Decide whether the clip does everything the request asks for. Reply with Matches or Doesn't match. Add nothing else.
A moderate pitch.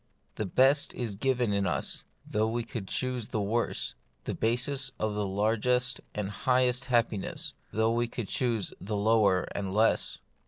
Doesn't match